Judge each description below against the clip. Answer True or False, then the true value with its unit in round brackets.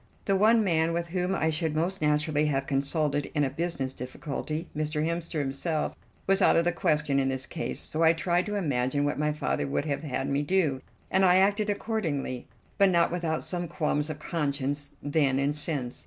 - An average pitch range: True (3.4 semitones)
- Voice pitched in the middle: True (155 Hz)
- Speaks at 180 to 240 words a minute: True (200 wpm)